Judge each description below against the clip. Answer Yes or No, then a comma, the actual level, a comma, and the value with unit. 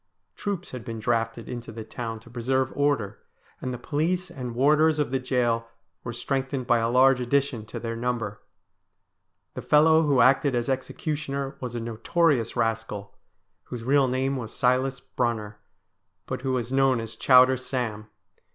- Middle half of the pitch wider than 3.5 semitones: No, average, 2.9 semitones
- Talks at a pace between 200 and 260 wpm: No, average, 165 wpm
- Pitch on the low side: Yes, low, 125 Hz